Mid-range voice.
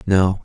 No: very low, 95 Hz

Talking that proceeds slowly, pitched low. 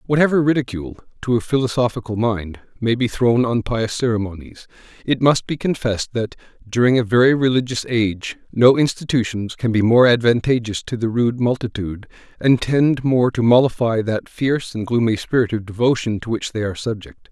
No: average, 170 wpm; low, 120 Hz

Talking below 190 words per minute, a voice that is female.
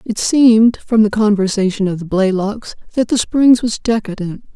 Yes: average, 170 wpm; female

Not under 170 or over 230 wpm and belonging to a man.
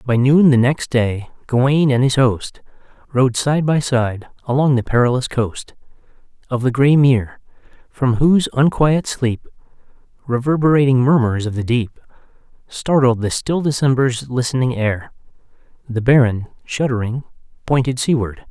No: slow, 135 wpm; male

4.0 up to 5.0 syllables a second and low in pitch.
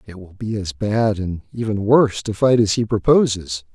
Yes: 4.9 syllables/s; low, 105 Hz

